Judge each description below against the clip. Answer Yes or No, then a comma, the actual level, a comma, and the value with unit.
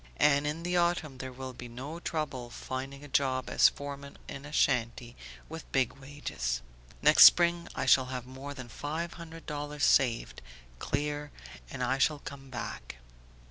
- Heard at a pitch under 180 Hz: Yes, medium, 140 Hz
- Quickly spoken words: No, average, 165 wpm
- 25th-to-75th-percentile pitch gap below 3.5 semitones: Yes, narrow, 2.5 semitones